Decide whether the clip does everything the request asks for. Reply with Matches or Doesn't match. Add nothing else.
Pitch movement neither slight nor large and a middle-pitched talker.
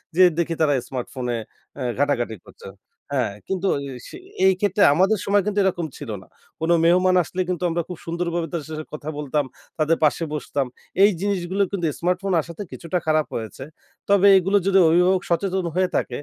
Matches